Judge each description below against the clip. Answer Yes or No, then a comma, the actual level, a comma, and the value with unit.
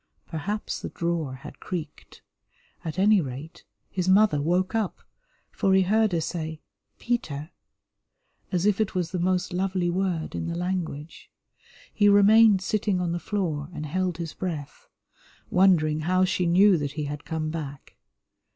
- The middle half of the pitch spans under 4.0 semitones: Yes, average, 3.5 semitones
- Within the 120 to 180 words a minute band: Yes, average, 155 wpm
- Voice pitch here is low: No, medium, 175 Hz